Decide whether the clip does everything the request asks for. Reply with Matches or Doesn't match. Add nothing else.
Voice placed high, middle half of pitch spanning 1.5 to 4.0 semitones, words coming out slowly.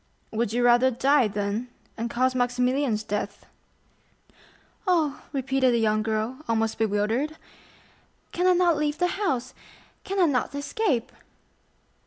Doesn't match